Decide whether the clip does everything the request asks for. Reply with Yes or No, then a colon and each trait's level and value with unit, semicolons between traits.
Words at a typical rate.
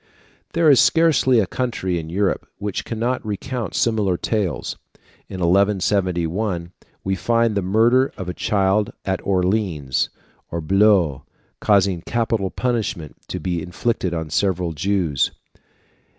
No: slow, 125 wpm